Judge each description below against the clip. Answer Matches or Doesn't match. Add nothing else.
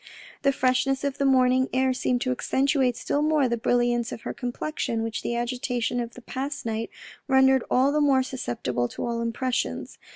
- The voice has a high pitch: Matches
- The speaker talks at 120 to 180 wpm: Doesn't match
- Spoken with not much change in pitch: Matches